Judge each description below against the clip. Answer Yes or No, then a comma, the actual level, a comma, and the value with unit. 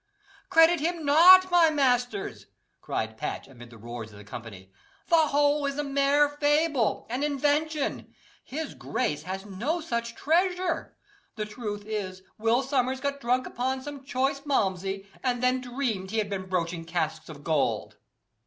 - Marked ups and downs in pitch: Yes, wide, 7.2 semitones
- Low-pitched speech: No, very high, 255 Hz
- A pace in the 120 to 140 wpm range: No, average, 155 wpm